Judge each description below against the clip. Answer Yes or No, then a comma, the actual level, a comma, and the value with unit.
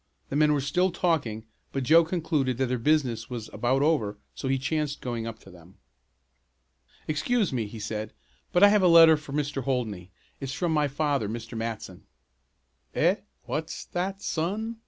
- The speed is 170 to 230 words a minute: Yes, average, 175 wpm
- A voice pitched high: No, medium, 140 Hz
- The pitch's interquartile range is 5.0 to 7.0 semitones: Yes, wide, 5.6 semitones